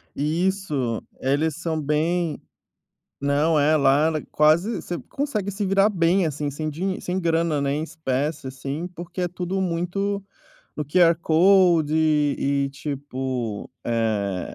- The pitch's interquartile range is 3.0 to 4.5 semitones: Yes, average, 3.9 semitones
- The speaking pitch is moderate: Yes, medium, 155 Hz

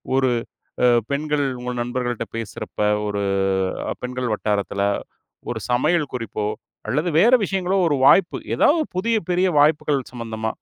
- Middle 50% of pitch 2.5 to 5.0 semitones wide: No, wide, 5.6 semitones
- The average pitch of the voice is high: No, low, 130 Hz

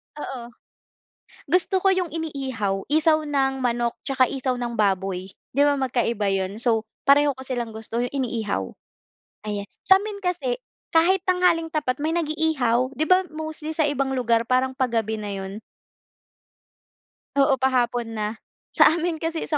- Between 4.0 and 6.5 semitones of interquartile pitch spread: Yes, average, 5.2 semitones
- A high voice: Yes, very high, 265 Hz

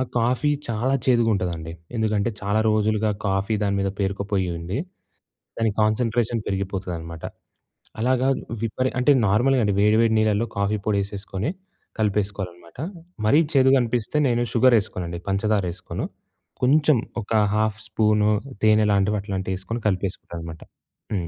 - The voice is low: Yes, low, 105 Hz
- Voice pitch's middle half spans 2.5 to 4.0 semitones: Yes, average, 2.9 semitones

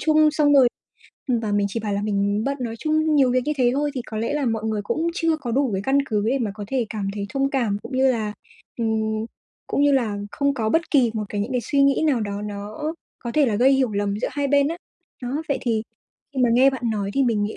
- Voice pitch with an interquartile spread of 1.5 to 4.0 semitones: No, average, 4.6 semitones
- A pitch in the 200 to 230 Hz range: No, high, 245 Hz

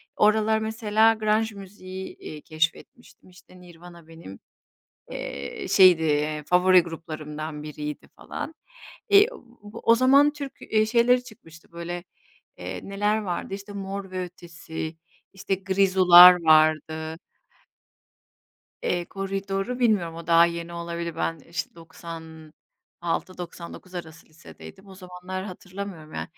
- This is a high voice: No, medium, 180 Hz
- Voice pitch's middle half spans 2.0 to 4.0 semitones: Yes, average, 3.4 semitones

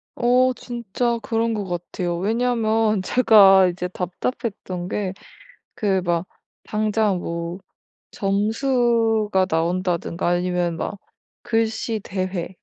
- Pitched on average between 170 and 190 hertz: No, high, 200 Hz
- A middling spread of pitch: Yes, average, 3.9 semitones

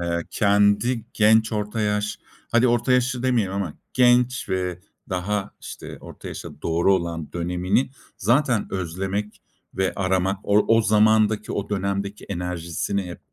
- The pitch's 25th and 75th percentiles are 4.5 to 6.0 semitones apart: No, average, 3.1 semitones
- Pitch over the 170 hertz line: No, low, 100 Hz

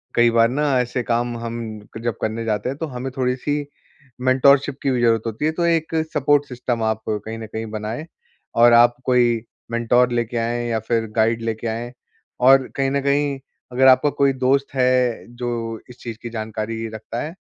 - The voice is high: No, low, 120 Hz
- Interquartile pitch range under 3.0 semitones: Yes, narrow, 2.6 semitones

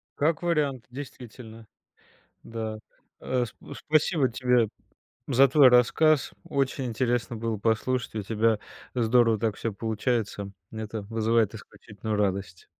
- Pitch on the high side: No, low, 115 Hz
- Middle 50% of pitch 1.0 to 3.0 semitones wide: Yes, average, 2.7 semitones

